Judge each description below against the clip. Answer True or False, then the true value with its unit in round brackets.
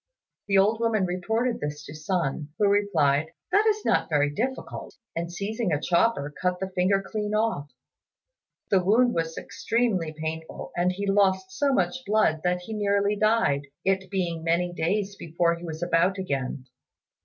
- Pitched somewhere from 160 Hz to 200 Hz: True (185 Hz)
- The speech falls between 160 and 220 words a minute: True (165 wpm)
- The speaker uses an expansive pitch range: False (4.3 semitones)